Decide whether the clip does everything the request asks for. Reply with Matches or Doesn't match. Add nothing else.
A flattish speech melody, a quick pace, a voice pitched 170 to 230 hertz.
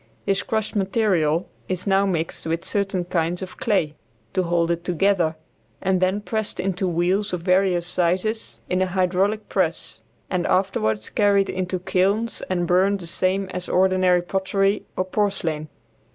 Doesn't match